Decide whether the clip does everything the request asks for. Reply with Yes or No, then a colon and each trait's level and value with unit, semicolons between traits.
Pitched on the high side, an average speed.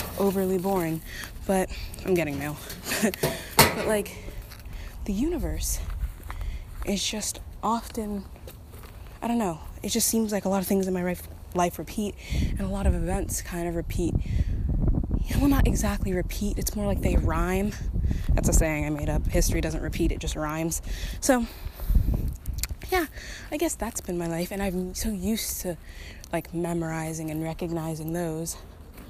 No: medium, 170 Hz; average, 160 wpm